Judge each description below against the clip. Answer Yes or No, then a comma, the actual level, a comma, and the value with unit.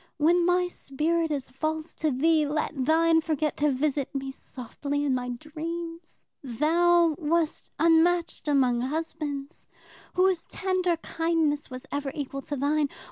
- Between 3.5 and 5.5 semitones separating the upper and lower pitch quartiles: No, average, 2.9 semitones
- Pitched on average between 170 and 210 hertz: No, very high, 310 Hz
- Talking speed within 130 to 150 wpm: Yes, slow, 135 wpm